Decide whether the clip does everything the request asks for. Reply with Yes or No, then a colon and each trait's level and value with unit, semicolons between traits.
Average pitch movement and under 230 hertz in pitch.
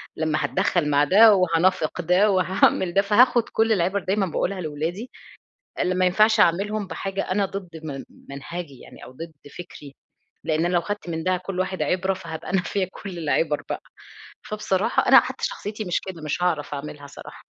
Yes: average, 3.4 semitones; medium, 185 Hz